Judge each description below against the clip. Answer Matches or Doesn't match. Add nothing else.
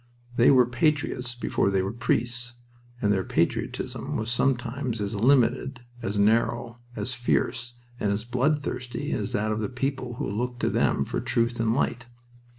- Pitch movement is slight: Matches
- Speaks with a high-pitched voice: Doesn't match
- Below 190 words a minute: Matches